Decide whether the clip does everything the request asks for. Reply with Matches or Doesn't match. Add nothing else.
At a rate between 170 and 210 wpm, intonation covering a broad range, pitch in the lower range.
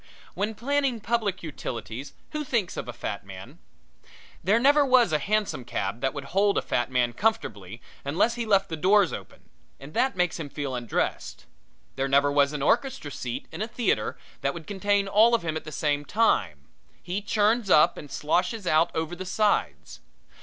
Doesn't match